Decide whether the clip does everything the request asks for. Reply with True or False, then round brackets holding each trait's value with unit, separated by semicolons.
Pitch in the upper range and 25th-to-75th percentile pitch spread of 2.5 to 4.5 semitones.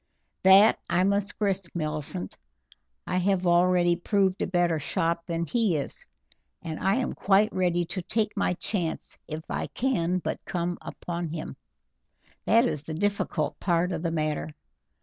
False (175 Hz; 2.9 semitones)